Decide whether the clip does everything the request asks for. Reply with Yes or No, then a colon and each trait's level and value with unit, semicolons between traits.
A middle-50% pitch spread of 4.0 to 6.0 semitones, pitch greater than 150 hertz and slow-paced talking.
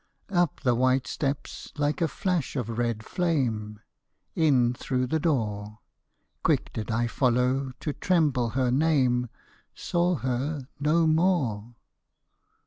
No: average, 4.7 semitones; low, 130 Hz; slow, 130 wpm